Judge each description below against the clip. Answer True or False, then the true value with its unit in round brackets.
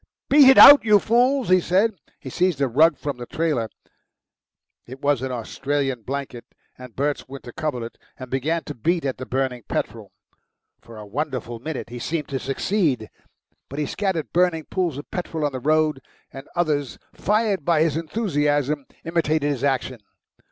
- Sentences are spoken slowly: False (170 wpm)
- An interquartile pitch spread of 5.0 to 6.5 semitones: False (4.3 semitones)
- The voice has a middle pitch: True (145 Hz)